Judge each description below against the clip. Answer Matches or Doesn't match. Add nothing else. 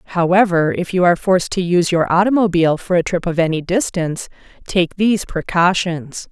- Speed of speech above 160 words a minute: Matches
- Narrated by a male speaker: Doesn't match